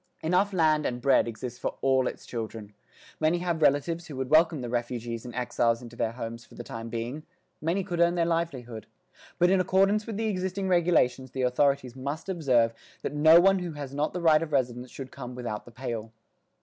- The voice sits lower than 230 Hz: Yes, medium, 140 Hz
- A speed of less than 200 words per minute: No, fast, 205 wpm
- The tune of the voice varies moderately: No, wide, 5.9 semitones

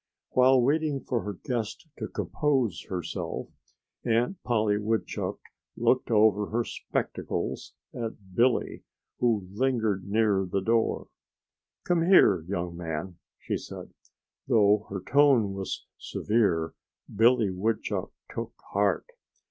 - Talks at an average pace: No, slow, 115 wpm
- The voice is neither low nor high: No, low, 110 Hz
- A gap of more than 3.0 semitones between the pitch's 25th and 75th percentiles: Yes, average, 4.1 semitones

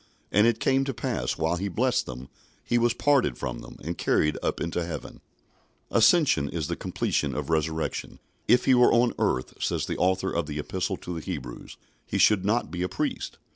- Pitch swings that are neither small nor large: No, wide, 7.2 semitones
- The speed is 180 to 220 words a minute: Yes, average, 200 wpm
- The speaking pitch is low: Yes, very low, 90 Hz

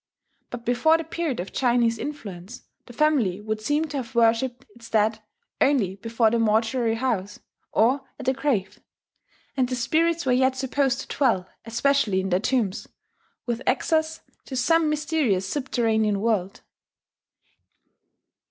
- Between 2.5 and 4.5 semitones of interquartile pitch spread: Yes, average, 4.1 semitones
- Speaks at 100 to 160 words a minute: Yes, average, 145 wpm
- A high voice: Yes, high, 240 Hz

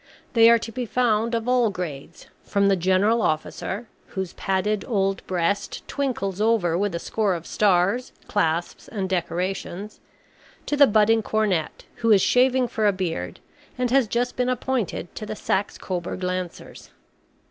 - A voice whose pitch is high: Yes, high, 205 Hz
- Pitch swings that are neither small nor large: Yes, average, 4.1 semitones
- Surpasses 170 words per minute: No, average, 160 wpm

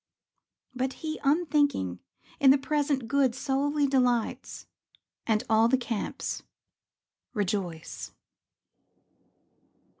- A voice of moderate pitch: No, very high, 265 Hz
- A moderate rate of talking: No, slow, 85 wpm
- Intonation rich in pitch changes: No, average, 4.2 semitones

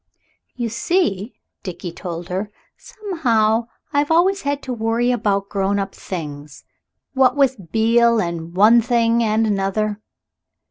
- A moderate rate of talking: No, slow, 130 wpm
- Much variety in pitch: No, average, 4.1 semitones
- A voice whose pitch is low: No, high, 225 Hz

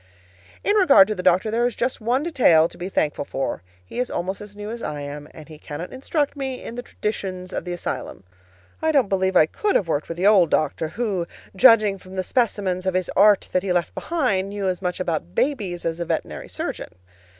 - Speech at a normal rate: No, fast, 225 wpm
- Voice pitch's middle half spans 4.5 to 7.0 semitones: Yes, average, 5.0 semitones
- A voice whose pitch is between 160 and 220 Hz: Yes, high, 190 Hz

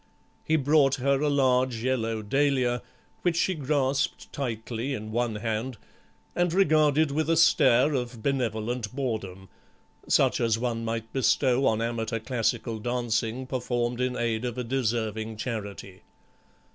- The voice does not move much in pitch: No, average, 3.3 semitones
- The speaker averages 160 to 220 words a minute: No, slow, 135 wpm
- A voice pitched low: Yes, low, 125 Hz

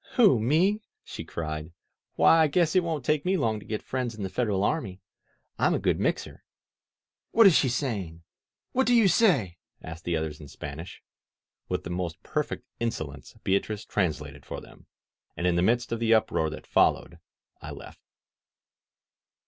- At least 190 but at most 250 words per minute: No, average, 175 wpm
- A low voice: Yes, low, 110 Hz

